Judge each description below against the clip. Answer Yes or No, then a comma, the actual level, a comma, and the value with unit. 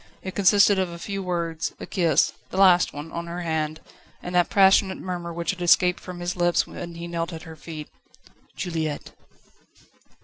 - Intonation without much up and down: Yes, narrow, 1.7 semitones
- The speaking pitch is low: No, medium, 175 Hz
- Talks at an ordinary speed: Yes, average, 180 wpm